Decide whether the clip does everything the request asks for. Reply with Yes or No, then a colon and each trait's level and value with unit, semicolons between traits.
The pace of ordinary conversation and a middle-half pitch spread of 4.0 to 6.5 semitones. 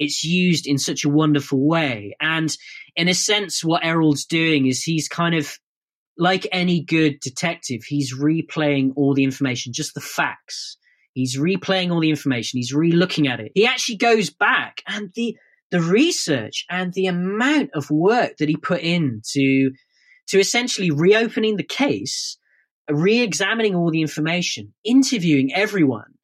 Yes: average, 160 wpm; average, 4.4 semitones